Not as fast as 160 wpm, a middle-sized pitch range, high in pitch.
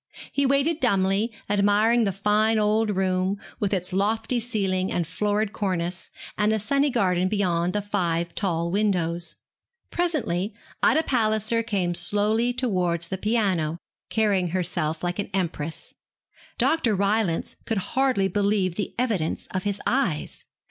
Yes: slow, 135 wpm; average, 3.4 semitones; high, 200 Hz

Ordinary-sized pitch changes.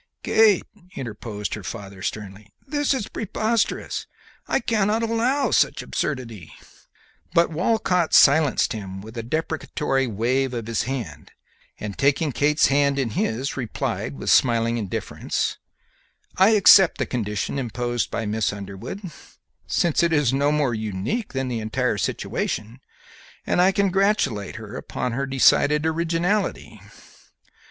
No: wide, 7.5 semitones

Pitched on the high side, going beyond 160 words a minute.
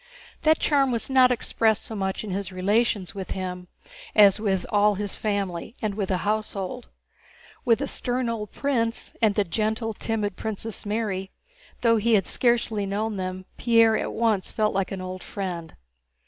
Yes: high, 210 Hz; average, 170 wpm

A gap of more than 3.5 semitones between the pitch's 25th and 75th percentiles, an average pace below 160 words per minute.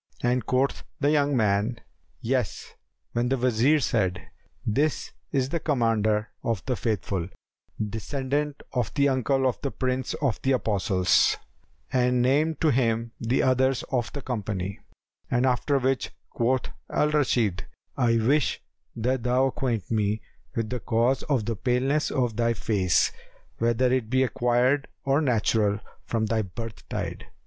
No: average, 3.0 semitones; average, 145 wpm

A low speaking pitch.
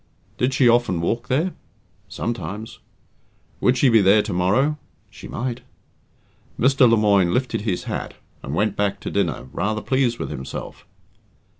Yes: low, 115 Hz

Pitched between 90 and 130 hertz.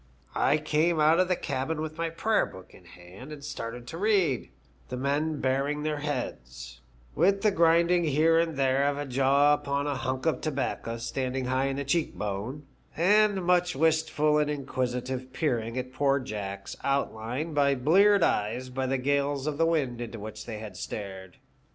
No: medium, 140 Hz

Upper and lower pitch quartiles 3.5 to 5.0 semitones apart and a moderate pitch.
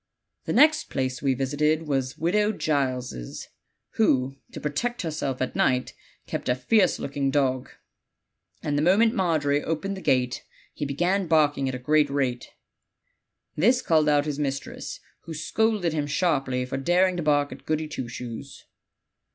Yes: average, 4.2 semitones; medium, 145 Hz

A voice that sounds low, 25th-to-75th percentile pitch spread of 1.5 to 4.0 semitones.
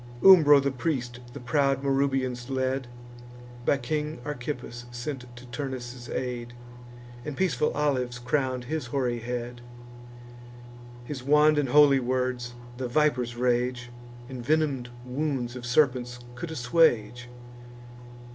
Yes: low, 130 Hz; average, 2.8 semitones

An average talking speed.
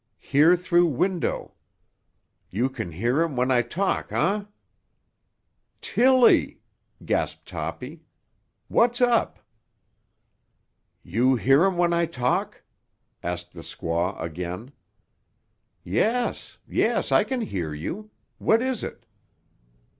No: slow, 105 wpm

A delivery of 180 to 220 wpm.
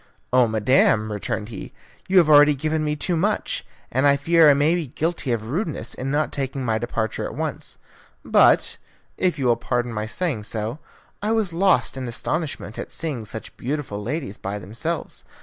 Yes: average, 185 wpm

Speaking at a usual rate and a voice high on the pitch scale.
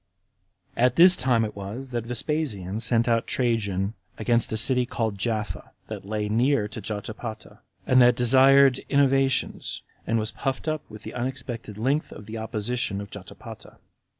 No: average, 160 wpm; low, 115 Hz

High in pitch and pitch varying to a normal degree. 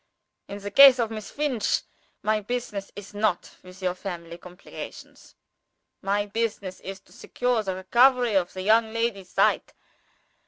Yes: high, 205 Hz; average, 3.5 semitones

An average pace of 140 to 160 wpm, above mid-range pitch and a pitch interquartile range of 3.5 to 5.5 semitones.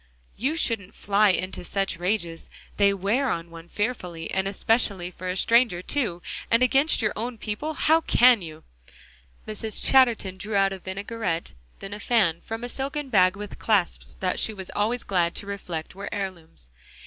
No: average, 170 wpm; high, 200 Hz; average, 4.1 semitones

